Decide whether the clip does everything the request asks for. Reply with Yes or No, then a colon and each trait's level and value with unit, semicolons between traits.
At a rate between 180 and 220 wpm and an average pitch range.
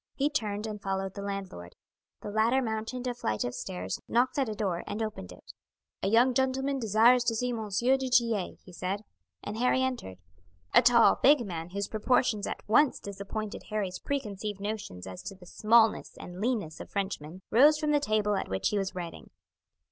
Yes: average, 190 wpm; average, 4.2 semitones